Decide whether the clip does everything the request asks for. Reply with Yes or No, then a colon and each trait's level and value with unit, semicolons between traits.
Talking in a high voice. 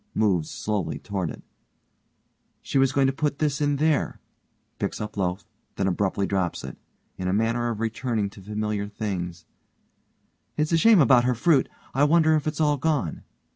No: low, 115 Hz